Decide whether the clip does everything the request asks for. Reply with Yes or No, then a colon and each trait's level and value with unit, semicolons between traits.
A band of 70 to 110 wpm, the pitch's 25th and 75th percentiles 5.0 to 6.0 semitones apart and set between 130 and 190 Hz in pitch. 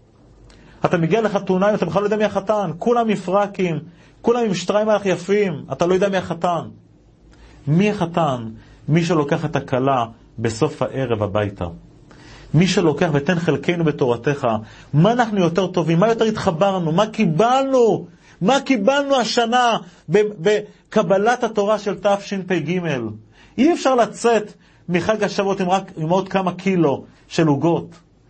No: average, 140 wpm; average, 5.3 semitones; medium, 185 Hz